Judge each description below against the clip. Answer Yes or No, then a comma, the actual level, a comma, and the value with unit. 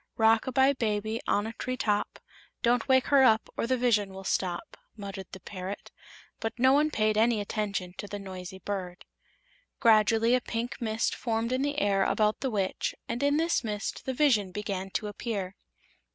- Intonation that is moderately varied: Yes, average, 3.5 semitones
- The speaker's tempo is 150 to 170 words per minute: No, average, 185 wpm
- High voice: Yes, high, 220 Hz